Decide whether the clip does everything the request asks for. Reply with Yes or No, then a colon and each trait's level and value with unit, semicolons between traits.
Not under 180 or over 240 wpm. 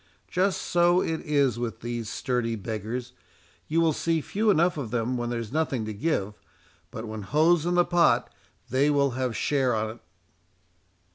No: average, 165 wpm